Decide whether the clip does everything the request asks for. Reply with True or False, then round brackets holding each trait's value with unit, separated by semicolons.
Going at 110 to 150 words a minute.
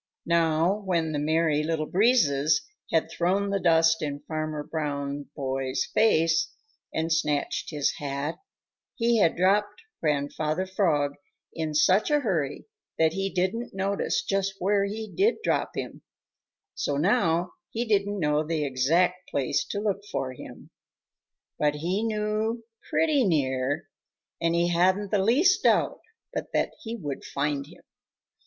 True (140 wpm)